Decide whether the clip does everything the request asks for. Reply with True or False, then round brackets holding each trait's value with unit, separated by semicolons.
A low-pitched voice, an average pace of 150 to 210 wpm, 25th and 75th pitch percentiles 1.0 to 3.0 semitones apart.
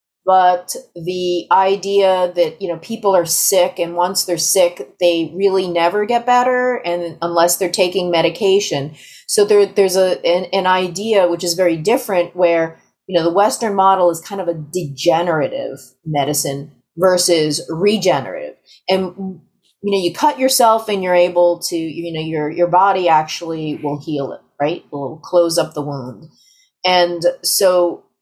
False (175 Hz; 160 wpm; 2.5 semitones)